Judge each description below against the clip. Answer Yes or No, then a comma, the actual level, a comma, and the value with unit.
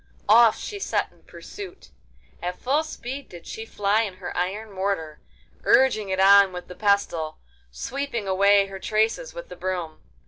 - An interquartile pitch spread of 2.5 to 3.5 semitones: No, average, 4.2 semitones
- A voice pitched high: Yes, high, 200 Hz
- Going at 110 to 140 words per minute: No, average, 165 wpm